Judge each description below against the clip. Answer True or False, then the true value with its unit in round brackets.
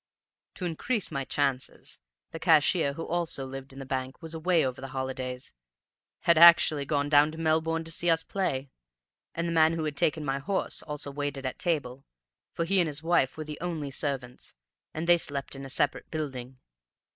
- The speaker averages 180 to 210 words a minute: True (190 wpm)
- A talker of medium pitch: True (150 Hz)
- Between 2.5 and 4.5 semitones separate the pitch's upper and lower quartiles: True (3.3 semitones)